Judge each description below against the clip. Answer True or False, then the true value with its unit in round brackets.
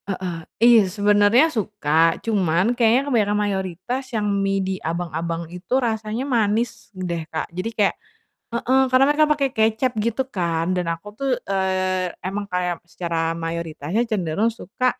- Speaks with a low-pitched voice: False (205 Hz)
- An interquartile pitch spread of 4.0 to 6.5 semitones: True (4.4 semitones)